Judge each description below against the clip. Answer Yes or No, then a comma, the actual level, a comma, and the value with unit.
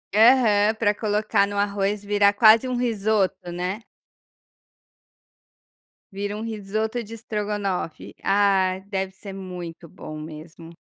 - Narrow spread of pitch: Yes, narrow, 2.2 semitones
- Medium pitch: No, high, 205 Hz